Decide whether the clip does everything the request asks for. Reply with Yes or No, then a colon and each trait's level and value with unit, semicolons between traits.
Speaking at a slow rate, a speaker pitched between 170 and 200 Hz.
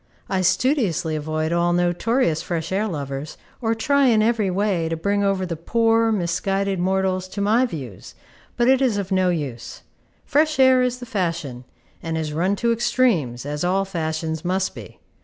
No: average, 175 wpm; medium, 185 Hz